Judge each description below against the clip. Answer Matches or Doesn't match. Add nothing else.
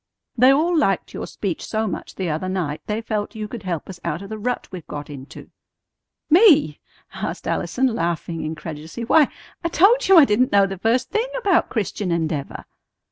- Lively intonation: Matches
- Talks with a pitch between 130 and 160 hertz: Doesn't match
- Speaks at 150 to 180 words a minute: Doesn't match